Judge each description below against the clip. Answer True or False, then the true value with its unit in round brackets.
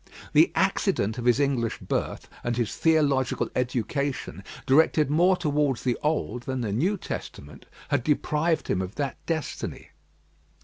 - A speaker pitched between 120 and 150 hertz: True (135 Hz)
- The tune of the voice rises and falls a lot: False (4.1 semitones)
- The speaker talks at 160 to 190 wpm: False (140 wpm)